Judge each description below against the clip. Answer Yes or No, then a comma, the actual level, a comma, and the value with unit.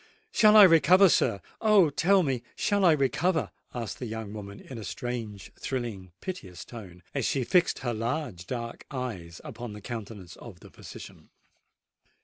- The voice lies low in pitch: Yes, low, 120 Hz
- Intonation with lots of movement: Yes, wide, 7.2 semitones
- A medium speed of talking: Yes, average, 155 wpm